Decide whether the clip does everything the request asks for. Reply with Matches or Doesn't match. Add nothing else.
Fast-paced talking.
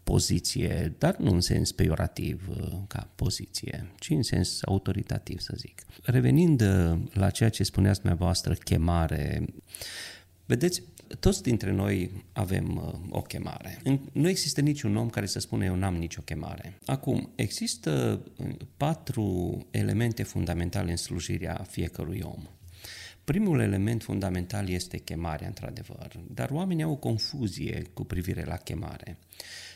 Doesn't match